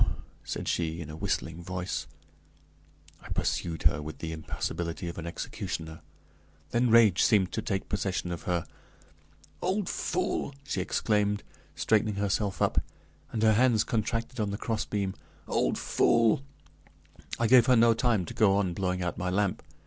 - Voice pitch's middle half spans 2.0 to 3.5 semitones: No, average, 4.4 semitones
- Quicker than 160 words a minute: No, average, 155 wpm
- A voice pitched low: Yes, low, 100 Hz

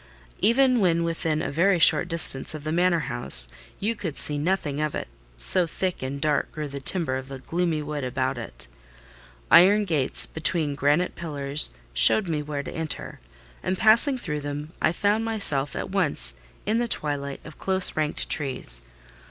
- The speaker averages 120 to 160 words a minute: No, average, 175 wpm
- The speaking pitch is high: No, medium, 155 Hz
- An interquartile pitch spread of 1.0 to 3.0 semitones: No, average, 4.4 semitones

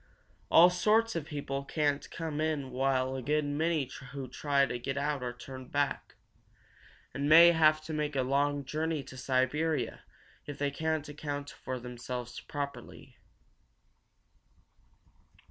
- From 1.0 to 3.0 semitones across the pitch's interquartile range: Yes, average, 2.7 semitones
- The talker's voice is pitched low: No, medium, 145 Hz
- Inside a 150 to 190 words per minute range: No, average, 140 wpm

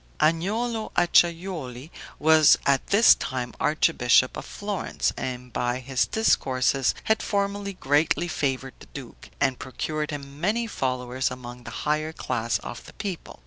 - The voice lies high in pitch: No, medium, 145 Hz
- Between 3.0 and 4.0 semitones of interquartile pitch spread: No, wide, 5.6 semitones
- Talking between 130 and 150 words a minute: Yes, average, 140 wpm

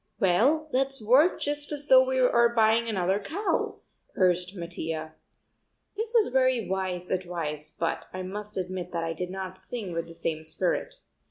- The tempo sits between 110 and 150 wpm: No, average, 165 wpm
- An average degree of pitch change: No, wide, 6.6 semitones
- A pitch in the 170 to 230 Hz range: Yes, high, 190 Hz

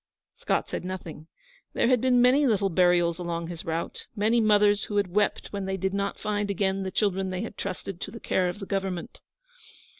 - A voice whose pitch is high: Yes, high, 195 Hz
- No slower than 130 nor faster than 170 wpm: No, fast, 205 wpm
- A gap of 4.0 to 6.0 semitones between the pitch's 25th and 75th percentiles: No, narrow, 2.6 semitones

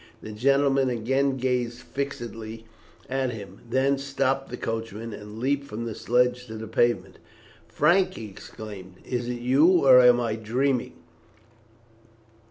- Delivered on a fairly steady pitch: No, average, 3.3 semitones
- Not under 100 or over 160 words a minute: Yes, average, 140 wpm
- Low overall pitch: Yes, low, 125 Hz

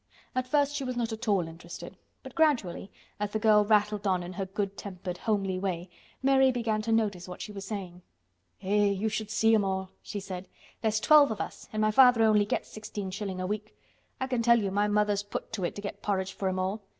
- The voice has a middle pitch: No, high, 205 Hz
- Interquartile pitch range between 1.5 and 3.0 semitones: Yes, narrow, 2.6 semitones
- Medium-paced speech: No, fast, 230 wpm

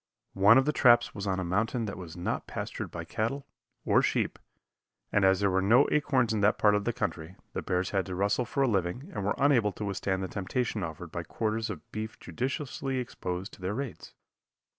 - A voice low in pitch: Yes, low, 105 Hz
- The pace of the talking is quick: Yes, fast, 215 wpm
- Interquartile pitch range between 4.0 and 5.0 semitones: Yes, average, 4.4 semitones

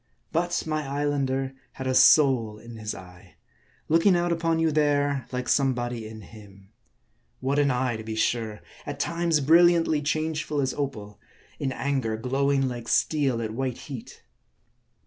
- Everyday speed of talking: Yes, average, 150 wpm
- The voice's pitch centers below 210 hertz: Yes, low, 135 Hz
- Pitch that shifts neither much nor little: Yes, average, 4.6 semitones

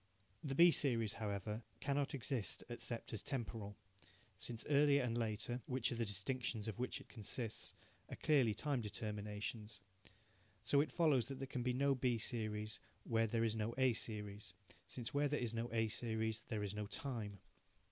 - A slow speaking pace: No, average, 175 wpm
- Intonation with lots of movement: No, average, 3.5 semitones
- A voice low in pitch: Yes, low, 115 Hz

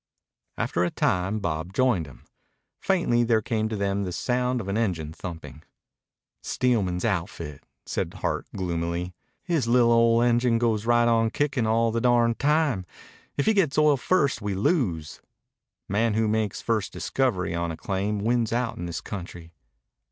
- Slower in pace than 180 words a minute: Yes, average, 165 wpm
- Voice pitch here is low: Yes, low, 110 Hz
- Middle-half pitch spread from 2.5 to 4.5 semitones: No, average, 5.0 semitones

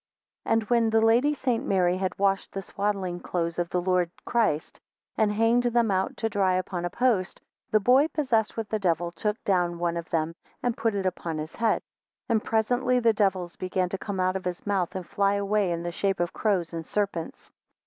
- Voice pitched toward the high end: Yes, high, 195 Hz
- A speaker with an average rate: No, fast, 215 wpm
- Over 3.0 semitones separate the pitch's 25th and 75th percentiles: Yes, average, 4.0 semitones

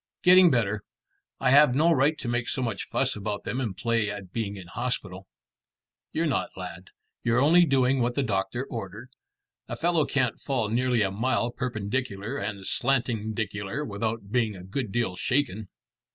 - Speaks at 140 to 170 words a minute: Yes, average, 165 wpm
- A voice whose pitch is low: Yes, low, 115 Hz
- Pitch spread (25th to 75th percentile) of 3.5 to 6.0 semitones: Yes, average, 4.3 semitones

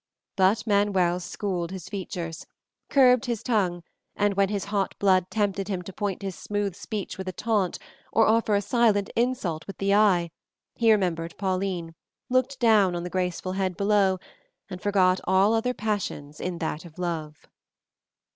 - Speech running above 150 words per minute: Yes, average, 165 wpm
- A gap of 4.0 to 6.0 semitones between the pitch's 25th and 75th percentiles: No, average, 2.7 semitones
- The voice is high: Yes, high, 195 Hz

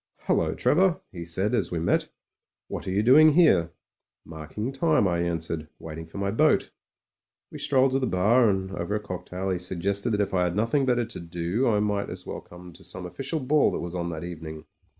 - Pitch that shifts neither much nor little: No, wide, 5.7 semitones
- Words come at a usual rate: No, fast, 210 wpm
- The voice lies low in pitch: Yes, very low, 95 Hz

